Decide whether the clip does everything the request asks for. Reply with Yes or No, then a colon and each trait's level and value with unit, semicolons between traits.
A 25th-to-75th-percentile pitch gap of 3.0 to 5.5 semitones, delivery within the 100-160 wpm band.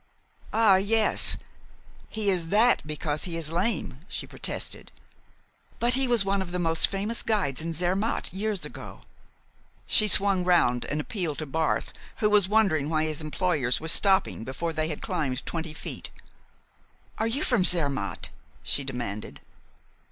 Yes: average, 5.2 semitones; average, 150 wpm